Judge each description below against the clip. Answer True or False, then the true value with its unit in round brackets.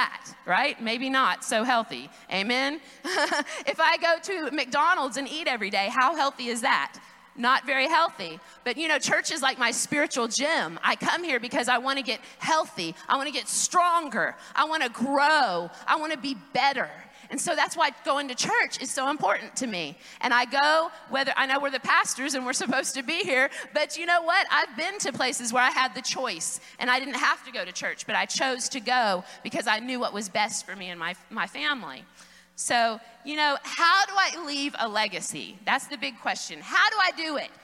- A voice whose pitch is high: True (270 Hz)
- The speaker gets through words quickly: True (220 wpm)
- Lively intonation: False (4.0 semitones)